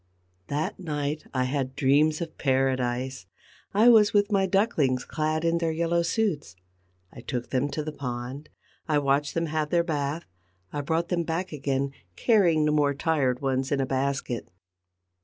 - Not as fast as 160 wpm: No, average, 165 wpm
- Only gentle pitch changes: No, average, 3.7 semitones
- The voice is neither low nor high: Yes, medium, 150 Hz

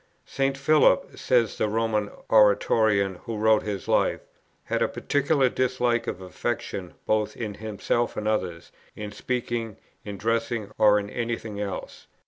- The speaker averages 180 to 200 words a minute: No, average, 145 wpm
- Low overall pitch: Yes, low, 110 Hz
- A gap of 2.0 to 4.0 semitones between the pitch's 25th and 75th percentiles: Yes, narrow, 2.5 semitones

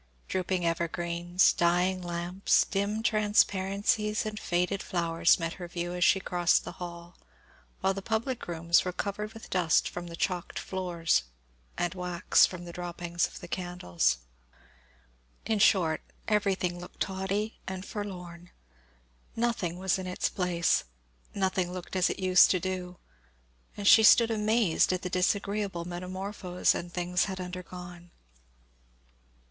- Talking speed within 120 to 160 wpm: Yes, average, 140 wpm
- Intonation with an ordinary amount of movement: No, narrow, 2.1 semitones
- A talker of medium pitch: Yes, medium, 180 Hz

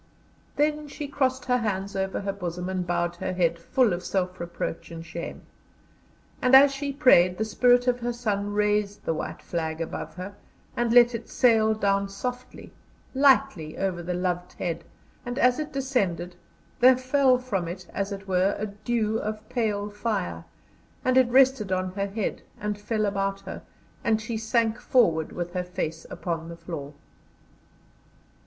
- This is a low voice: No, high, 205 Hz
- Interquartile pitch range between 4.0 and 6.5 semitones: Yes, average, 5.3 semitones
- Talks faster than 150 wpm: Yes, average, 170 wpm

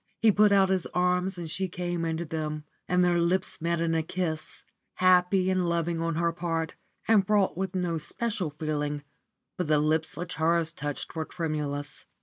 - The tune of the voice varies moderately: No, narrow, 2.3 semitones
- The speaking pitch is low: No, medium, 170 Hz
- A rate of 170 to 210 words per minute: Yes, average, 180 wpm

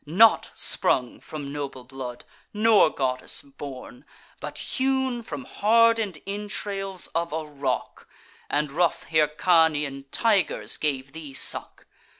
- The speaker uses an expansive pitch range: Yes, wide, 6.9 semitones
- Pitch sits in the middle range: Yes, medium, 155 Hz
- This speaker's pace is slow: Yes, slow, 115 wpm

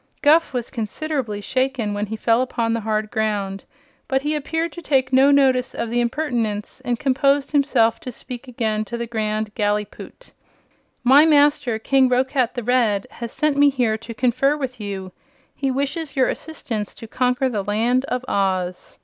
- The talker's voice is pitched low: No, high, 245 Hz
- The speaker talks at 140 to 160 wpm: No, average, 175 wpm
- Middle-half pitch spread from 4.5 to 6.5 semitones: No, average, 4.0 semitones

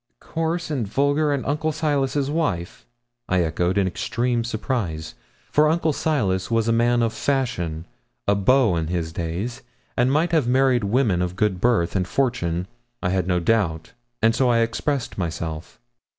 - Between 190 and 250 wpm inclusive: No, average, 165 wpm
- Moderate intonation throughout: No, wide, 7.3 semitones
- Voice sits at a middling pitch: No, low, 115 Hz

